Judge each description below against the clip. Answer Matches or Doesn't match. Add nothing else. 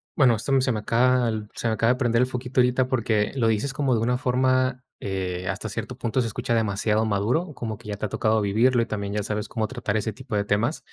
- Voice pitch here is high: Doesn't match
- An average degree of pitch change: Matches